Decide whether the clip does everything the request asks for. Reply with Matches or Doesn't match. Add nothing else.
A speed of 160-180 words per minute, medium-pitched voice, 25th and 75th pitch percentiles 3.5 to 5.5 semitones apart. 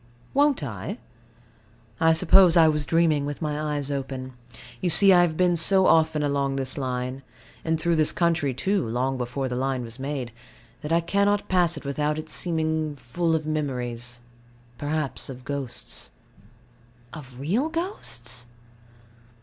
Doesn't match